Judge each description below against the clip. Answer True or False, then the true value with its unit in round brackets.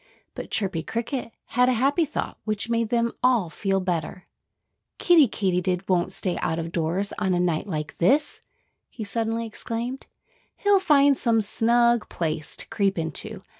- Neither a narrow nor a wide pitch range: True (5.0 semitones)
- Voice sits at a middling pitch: False (215 Hz)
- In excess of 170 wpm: False (160 wpm)